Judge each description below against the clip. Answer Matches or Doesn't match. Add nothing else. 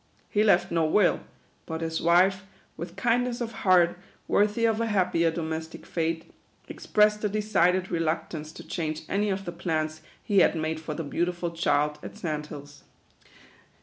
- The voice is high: Doesn't match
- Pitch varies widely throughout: Doesn't match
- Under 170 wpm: Matches